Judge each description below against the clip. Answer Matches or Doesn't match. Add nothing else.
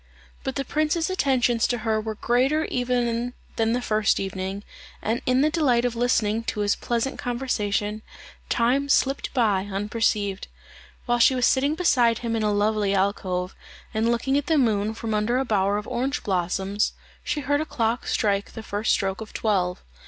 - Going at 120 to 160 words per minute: Doesn't match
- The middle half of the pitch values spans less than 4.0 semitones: Matches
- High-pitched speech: Matches